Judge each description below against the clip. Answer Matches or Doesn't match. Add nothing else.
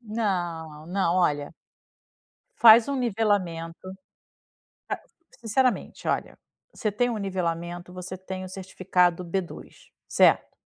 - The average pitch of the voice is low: Doesn't match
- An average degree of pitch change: Matches